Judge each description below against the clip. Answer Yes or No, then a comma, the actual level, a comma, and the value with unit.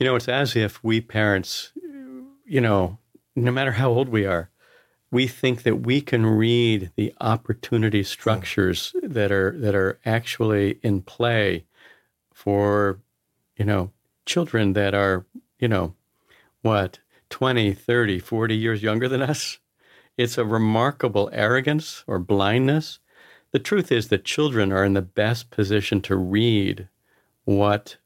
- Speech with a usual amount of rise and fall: Yes, average, 3.7 semitones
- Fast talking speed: No, average, 140 wpm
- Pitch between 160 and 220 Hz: No, low, 110 Hz